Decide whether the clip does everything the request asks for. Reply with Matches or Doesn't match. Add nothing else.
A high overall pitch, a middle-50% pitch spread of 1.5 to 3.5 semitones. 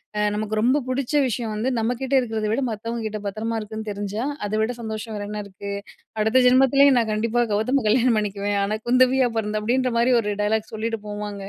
Matches